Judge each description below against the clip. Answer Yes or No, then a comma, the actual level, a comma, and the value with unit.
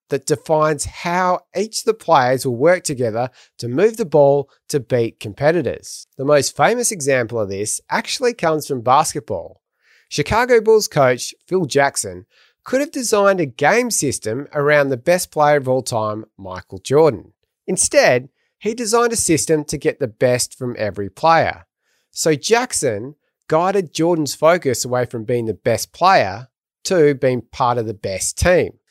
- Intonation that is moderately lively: No, wide, 6.1 semitones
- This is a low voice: No, medium, 150 Hz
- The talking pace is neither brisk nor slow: Yes, average, 160 wpm